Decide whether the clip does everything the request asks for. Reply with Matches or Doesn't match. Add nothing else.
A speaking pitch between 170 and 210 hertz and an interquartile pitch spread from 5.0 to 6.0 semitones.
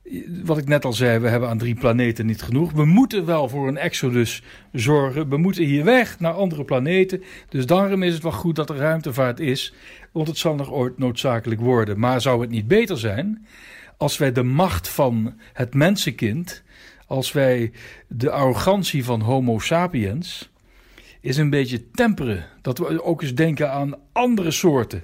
Doesn't match